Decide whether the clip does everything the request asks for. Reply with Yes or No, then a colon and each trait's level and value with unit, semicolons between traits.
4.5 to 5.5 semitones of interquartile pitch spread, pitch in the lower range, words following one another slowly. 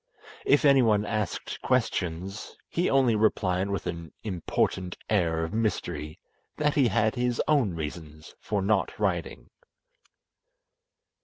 Yes: average, 5.0 semitones; low, 105 Hz; slow, 120 wpm